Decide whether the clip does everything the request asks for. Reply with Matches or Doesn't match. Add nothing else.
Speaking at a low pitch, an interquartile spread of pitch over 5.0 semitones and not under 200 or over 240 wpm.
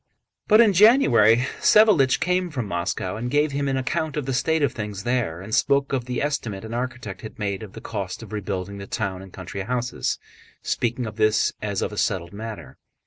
Matches